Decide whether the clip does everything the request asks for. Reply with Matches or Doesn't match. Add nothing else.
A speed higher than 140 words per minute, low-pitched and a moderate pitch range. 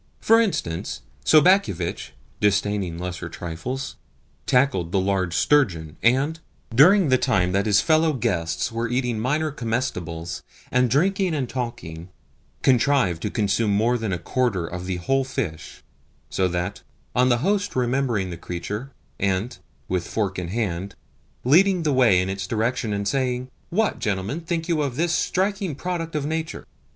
Doesn't match